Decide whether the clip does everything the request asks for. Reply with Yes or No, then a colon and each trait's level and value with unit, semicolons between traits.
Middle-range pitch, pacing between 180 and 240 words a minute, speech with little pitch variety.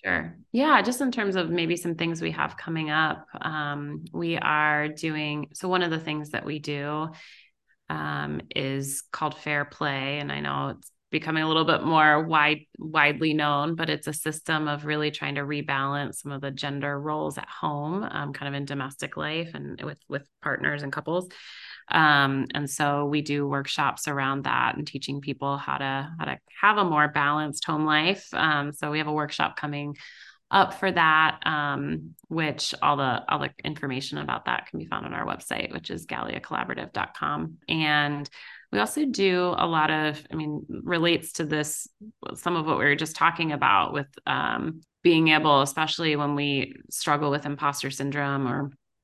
Yes: medium, 150 Hz; average, 185 wpm; narrow, 2.0 semitones